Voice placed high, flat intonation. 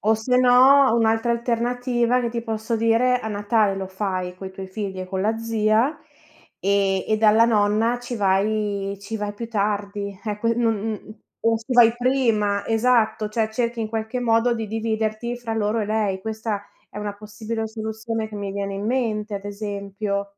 Yes: high, 220 Hz; narrow, 2.1 semitones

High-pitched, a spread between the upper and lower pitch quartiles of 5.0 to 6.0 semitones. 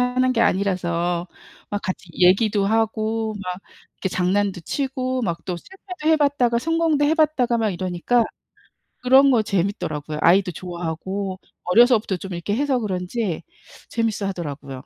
Yes: high, 205 Hz; wide, 5.6 semitones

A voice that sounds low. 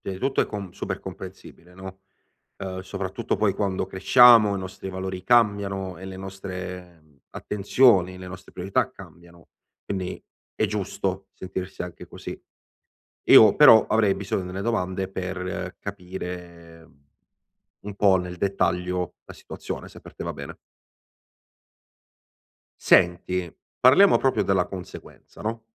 Yes: very low, 95 Hz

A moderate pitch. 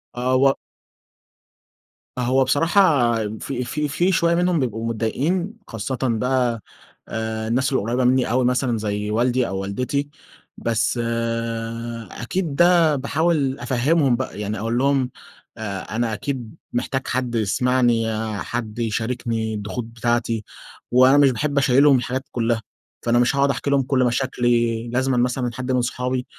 No: low, 125 Hz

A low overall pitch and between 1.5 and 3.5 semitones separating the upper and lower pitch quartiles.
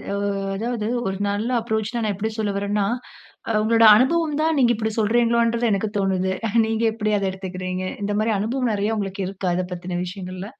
No: high, 215 Hz; average, 3.1 semitones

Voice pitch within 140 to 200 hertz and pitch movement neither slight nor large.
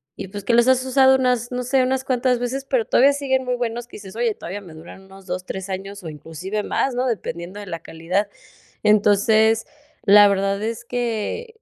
No: high, 220 Hz; average, 4.4 semitones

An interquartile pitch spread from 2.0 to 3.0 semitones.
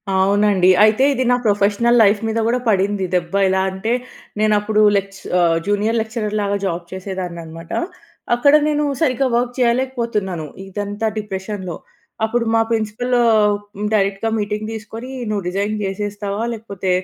Yes: average, 2.7 semitones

